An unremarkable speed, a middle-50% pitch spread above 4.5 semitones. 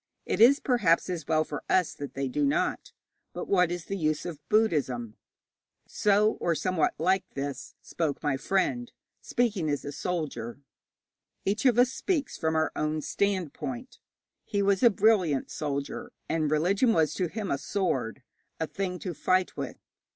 Yes: average, 165 wpm; average, 5.1 semitones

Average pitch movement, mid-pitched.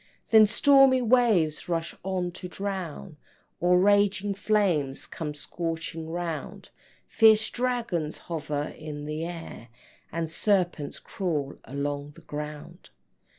Yes: average, 4.9 semitones; medium, 175 Hz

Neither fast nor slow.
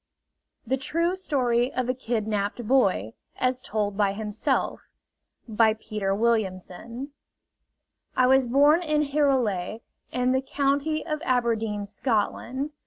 No: slow, 115 wpm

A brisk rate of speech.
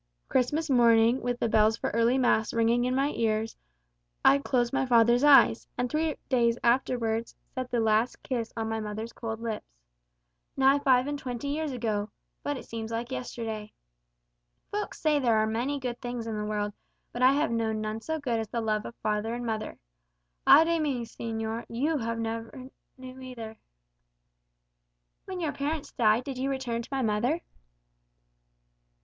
No: average, 175 wpm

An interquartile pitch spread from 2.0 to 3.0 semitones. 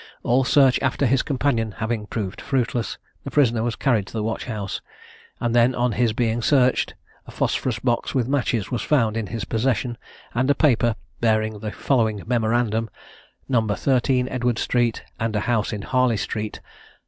Yes: narrow, 2.5 semitones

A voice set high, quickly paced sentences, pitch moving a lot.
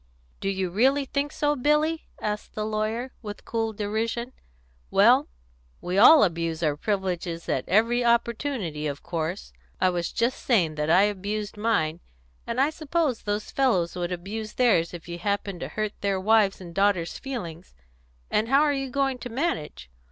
No: high, 210 Hz; average, 165 wpm; wide, 5.8 semitones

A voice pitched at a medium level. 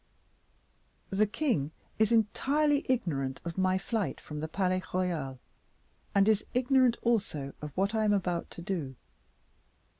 No: high, 195 Hz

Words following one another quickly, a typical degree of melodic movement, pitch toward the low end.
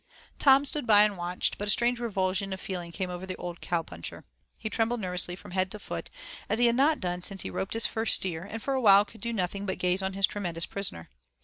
No: fast, 250 wpm; average, 3.8 semitones; high, 195 Hz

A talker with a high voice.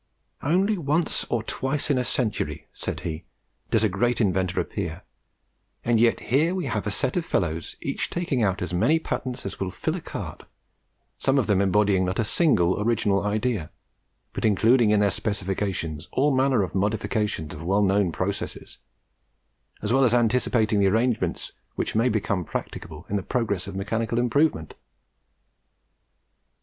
No: low, 105 Hz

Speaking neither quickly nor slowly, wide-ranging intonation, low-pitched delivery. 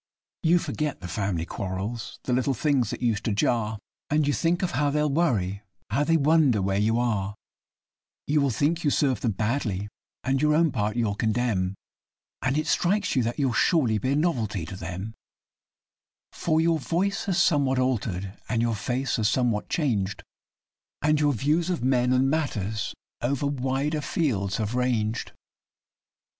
Yes: average, 165 wpm; wide, 5.9 semitones; low, 125 Hz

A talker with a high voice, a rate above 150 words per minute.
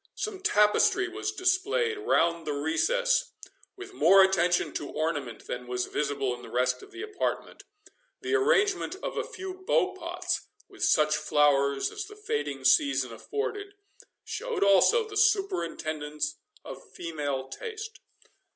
No: high, 195 Hz; average, 140 wpm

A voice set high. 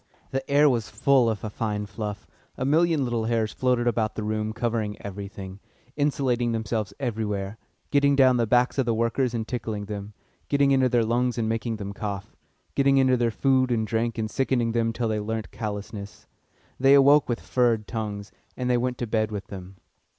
No: low, 115 Hz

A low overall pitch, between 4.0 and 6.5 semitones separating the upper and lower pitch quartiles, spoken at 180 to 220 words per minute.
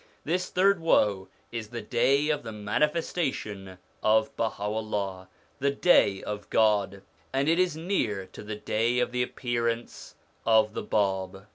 No: low, 110 Hz; average, 5.2 semitones; average, 145 wpm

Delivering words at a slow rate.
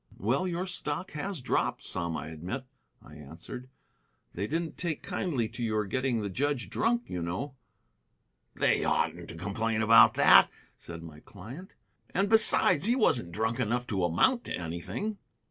No: average, 160 wpm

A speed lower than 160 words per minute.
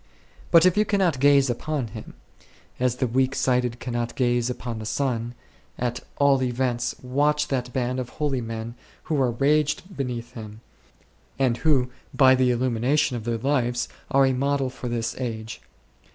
No: average, 165 wpm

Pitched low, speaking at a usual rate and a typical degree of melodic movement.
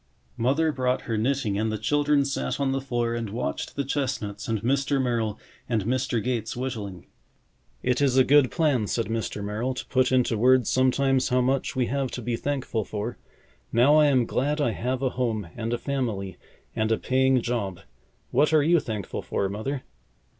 Yes: low, 125 Hz; average, 190 wpm; average, 3.3 semitones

